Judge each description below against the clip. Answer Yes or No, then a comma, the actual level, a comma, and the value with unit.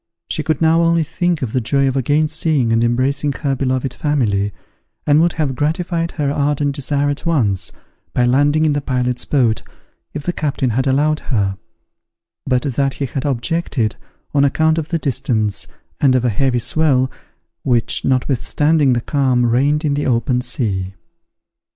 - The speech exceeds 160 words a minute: Yes, average, 170 wpm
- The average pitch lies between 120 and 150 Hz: Yes, low, 135 Hz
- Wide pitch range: No, average, 3.5 semitones